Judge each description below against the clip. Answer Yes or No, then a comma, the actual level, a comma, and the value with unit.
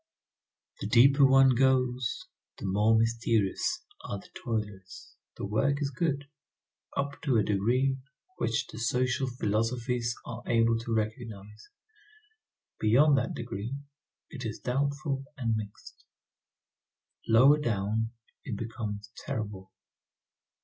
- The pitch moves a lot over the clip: No, average, 3.6 semitones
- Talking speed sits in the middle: No, slow, 115 wpm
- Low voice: Yes, low, 115 Hz